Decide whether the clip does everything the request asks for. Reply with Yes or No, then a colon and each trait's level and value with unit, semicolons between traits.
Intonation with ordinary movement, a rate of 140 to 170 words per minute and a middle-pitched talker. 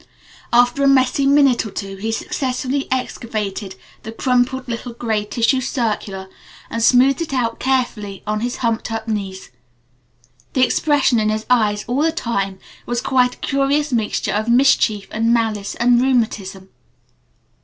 No: average, 3.4 semitones; average, 150 wpm; high, 235 Hz